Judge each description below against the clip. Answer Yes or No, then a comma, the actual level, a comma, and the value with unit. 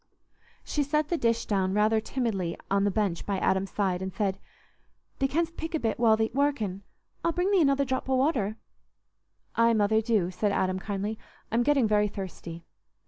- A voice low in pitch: No, high, 220 Hz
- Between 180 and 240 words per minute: Yes, average, 185 wpm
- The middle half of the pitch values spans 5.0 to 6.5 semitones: Yes, wide, 5.4 semitones